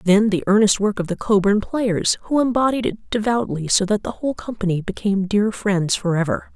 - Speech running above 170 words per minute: Yes, average, 190 wpm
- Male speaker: No, female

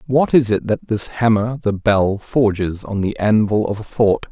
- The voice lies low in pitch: Yes, low, 110 Hz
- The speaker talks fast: No, average, 195 wpm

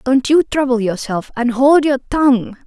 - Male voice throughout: No, female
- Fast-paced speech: No, average, 160 wpm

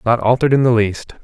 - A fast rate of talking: Yes, fast, 245 wpm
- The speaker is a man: Yes, male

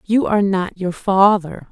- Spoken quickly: No, average, 175 wpm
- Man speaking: No, female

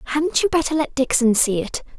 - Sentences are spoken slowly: No, fast, 210 wpm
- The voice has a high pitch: Yes, very high, 275 Hz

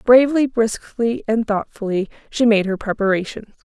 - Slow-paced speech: Yes, slow, 130 wpm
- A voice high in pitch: Yes, high, 225 Hz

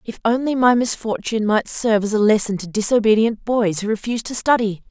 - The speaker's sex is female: Yes, female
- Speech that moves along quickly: No, average, 195 wpm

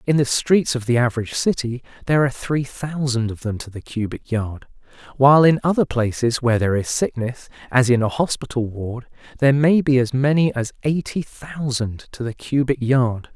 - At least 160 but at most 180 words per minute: No, average, 190 wpm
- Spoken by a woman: No, male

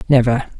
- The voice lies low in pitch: Yes, low, 125 Hz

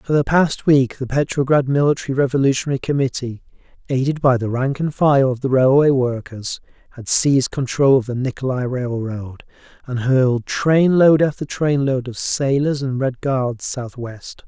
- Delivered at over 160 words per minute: No, average, 155 wpm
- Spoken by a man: Yes, male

